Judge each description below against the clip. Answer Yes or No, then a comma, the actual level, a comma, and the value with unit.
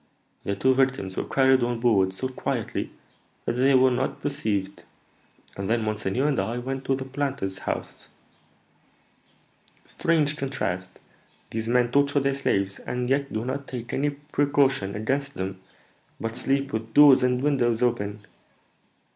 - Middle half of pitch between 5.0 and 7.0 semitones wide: No, average, 4.0 semitones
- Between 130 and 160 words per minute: Yes, average, 145 wpm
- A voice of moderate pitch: No, low, 125 Hz